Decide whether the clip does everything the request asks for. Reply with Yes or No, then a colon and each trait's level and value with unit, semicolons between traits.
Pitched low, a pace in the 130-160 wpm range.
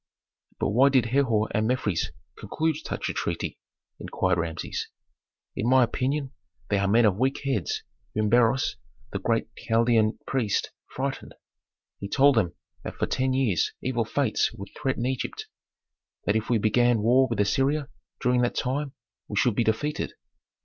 Yes: low, 120 Hz; average, 155 wpm